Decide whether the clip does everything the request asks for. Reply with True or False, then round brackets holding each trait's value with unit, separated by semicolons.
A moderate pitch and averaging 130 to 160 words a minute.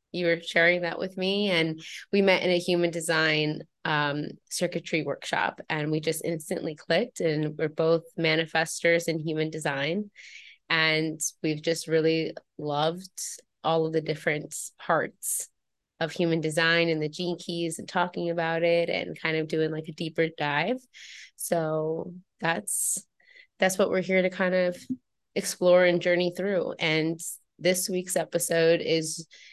True (165 Hz; 150 wpm)